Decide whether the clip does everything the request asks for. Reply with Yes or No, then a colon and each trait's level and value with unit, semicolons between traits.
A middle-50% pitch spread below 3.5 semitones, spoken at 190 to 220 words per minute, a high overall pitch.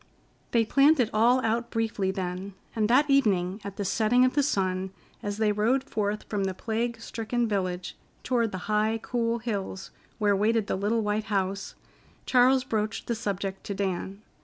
No: average, 3.0 semitones; average, 175 wpm; high, 215 Hz